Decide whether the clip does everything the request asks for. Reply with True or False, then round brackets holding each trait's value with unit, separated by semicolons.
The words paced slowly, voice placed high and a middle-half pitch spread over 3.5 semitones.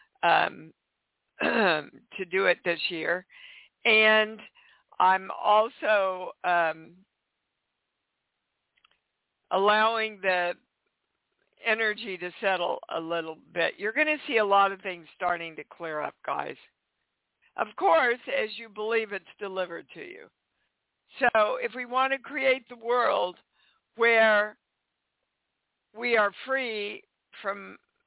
True (115 wpm; 210 Hz; 4.4 semitones)